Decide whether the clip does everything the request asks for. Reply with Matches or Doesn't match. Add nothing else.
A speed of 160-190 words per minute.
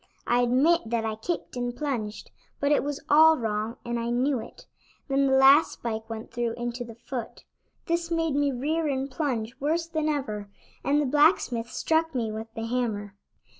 Matches